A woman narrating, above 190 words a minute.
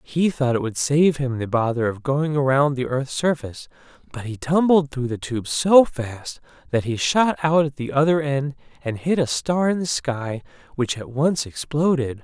No: male; average, 200 wpm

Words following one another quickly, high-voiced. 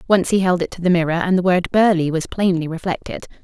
No: fast, 245 wpm; medium, 180 Hz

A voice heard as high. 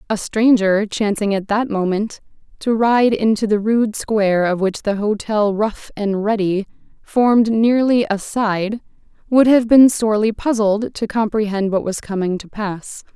Yes: high, 215 Hz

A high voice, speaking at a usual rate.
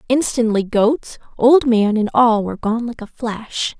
Yes: high, 230 Hz; average, 175 wpm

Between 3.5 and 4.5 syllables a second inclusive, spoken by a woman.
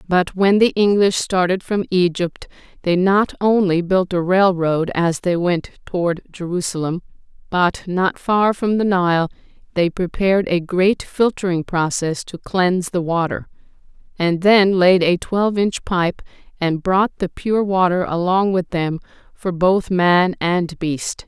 Yes: 4.1 syllables/s; female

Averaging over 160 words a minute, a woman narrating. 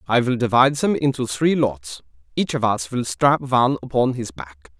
No: average, 200 wpm; male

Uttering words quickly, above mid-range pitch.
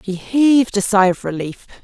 No: average, 195 wpm; high, 210 Hz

